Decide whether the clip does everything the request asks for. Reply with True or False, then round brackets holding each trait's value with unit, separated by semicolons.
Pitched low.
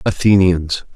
True (90 Hz)